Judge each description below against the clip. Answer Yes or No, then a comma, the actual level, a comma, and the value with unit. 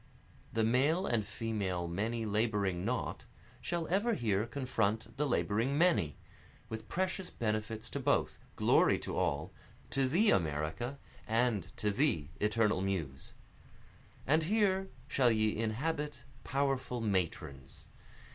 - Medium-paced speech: No, slow, 120 wpm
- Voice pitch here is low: Yes, low, 115 Hz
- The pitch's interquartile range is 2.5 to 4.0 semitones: No, wide, 5.6 semitones